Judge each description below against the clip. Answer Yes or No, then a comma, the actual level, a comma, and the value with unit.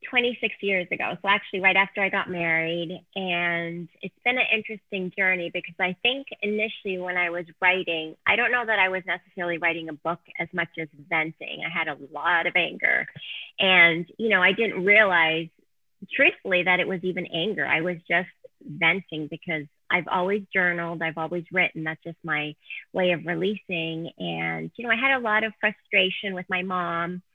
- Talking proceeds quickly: No, average, 185 wpm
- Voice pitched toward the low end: No, medium, 180 Hz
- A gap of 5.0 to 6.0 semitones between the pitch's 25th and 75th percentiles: No, average, 2.8 semitones